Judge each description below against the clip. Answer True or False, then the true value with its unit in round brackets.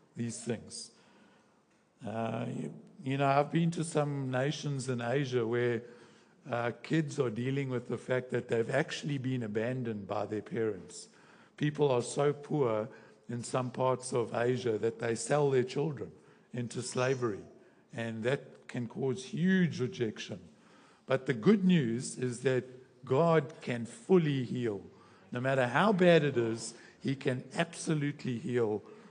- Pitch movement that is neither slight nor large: True (3.4 semitones)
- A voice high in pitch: False (130 Hz)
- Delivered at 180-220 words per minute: False (145 wpm)